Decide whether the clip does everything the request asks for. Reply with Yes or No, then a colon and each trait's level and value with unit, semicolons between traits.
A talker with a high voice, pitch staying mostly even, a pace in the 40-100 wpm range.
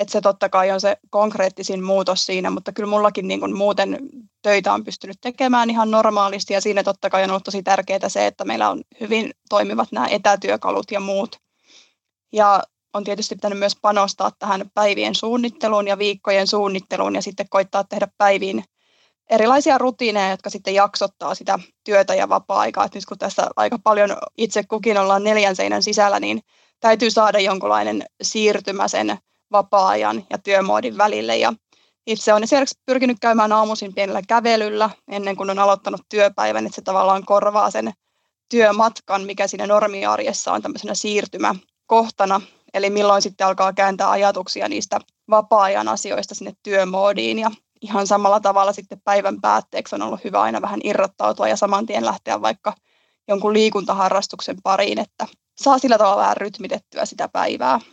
No: high, 205 Hz; narrow, 1.7 semitones; fast, 155 wpm